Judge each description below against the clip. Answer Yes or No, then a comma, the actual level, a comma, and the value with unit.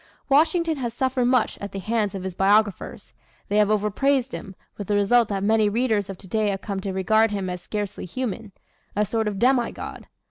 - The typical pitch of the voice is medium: No, high, 210 Hz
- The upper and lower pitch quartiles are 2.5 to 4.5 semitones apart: Yes, average, 3.2 semitones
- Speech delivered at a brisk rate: Yes, fast, 210 wpm